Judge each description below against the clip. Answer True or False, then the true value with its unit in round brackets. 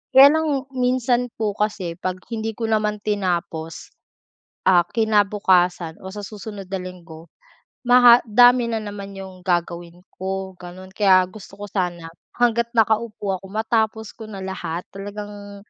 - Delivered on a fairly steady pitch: False (3.3 semitones)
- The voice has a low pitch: False (205 Hz)